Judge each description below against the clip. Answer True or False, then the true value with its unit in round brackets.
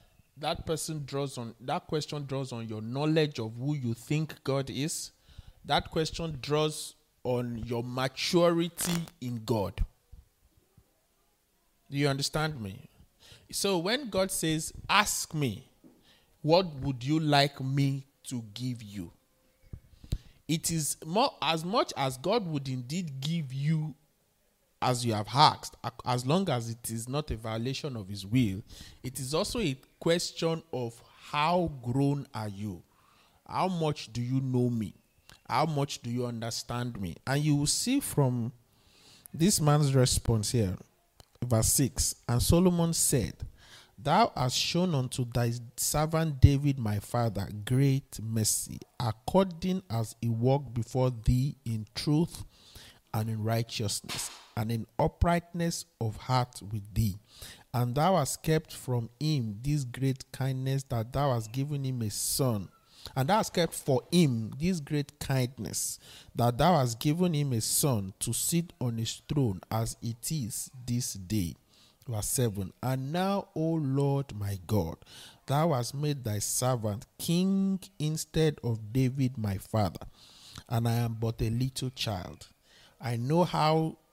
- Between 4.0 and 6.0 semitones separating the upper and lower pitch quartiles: True (4.9 semitones)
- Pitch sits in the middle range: False (130 Hz)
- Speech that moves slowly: False (145 wpm)